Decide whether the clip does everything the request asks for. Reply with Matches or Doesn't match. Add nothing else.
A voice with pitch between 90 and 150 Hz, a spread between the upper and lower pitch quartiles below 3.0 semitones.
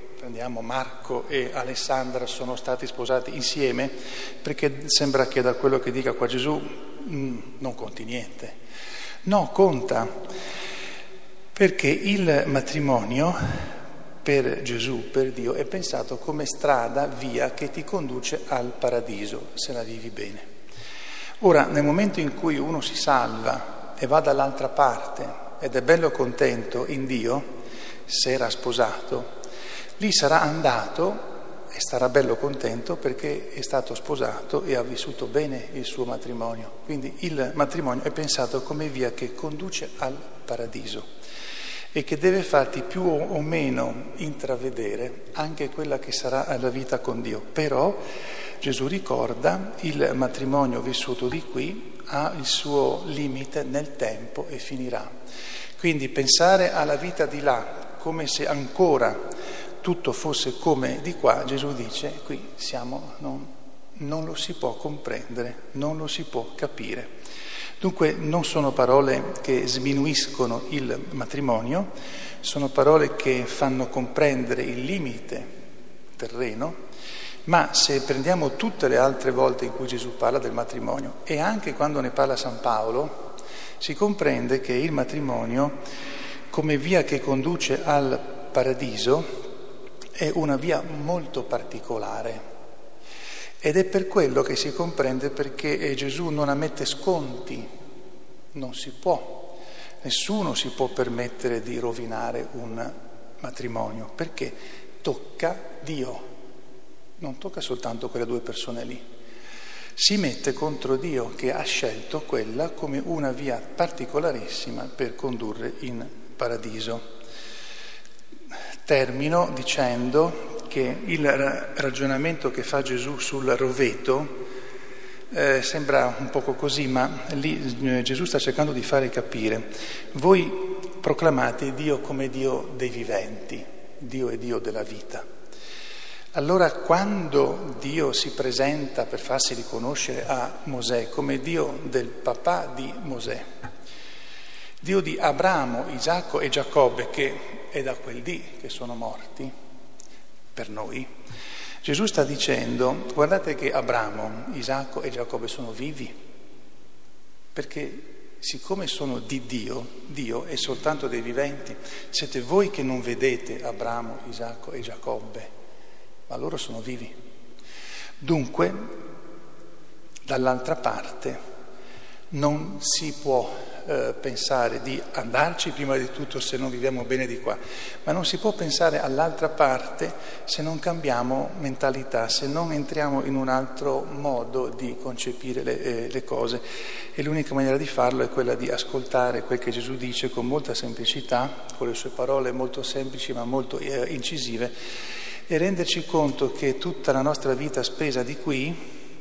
Doesn't match